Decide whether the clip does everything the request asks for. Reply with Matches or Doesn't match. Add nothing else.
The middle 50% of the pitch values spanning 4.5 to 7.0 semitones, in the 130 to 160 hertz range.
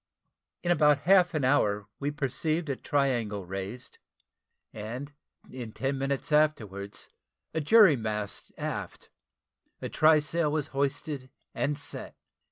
Matches